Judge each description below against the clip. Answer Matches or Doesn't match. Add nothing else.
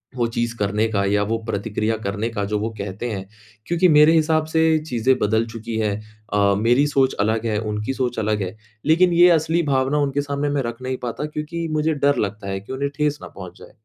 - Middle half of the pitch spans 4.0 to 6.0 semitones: Matches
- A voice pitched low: Matches